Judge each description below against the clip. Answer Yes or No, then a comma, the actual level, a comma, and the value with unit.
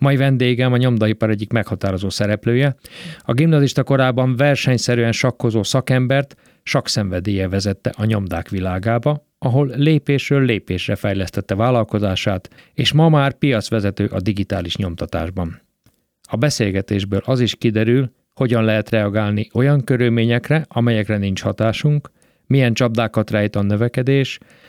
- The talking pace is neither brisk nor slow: Yes, average, 115 wpm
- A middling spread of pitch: Yes, average, 4.5 semitones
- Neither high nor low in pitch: No, low, 115 Hz